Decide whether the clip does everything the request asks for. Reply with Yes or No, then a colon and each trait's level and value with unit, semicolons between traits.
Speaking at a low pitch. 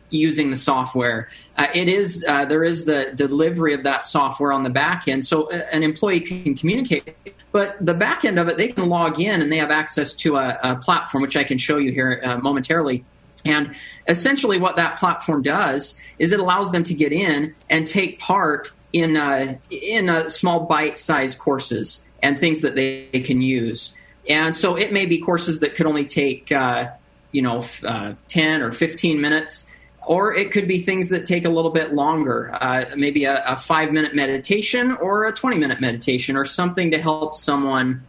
No: medium, 155 Hz